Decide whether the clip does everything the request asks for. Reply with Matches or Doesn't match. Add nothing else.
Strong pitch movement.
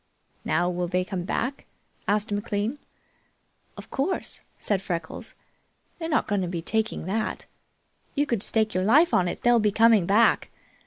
Doesn't match